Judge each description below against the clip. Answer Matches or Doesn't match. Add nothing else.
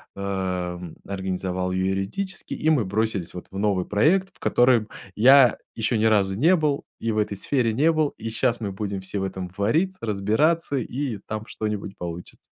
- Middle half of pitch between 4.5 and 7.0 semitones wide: Matches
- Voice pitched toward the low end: Matches